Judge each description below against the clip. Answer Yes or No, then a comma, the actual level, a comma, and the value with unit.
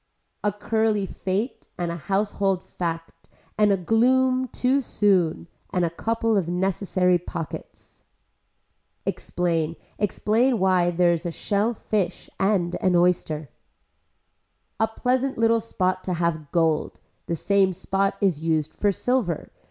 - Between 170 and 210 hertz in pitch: Yes, high, 190 Hz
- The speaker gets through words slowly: Yes, slow, 130 wpm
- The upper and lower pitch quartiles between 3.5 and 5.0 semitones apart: Yes, average, 3.9 semitones